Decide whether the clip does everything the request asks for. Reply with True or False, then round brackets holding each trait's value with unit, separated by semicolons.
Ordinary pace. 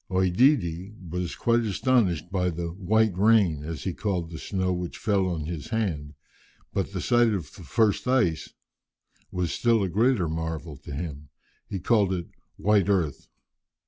True (160 wpm)